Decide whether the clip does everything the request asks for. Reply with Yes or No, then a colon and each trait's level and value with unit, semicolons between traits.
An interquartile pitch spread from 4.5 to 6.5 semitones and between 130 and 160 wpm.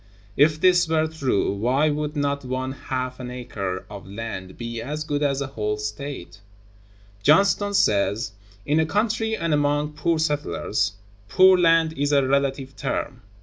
Yes: average, 5.1 semitones; average, 155 wpm